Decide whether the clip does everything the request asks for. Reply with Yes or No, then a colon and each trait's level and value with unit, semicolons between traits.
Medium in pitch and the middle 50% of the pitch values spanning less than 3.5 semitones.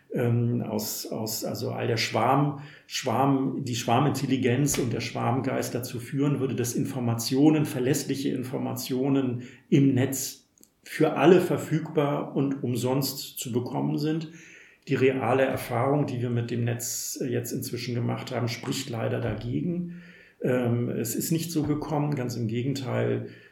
No: low, 130 Hz; average, 2.9 semitones